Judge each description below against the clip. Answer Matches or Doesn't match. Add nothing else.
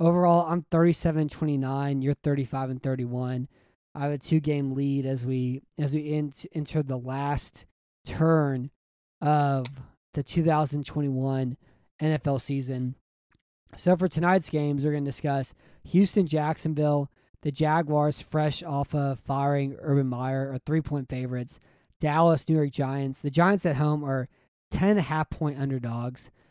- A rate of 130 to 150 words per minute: Matches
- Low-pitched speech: Doesn't match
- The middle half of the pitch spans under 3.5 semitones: Matches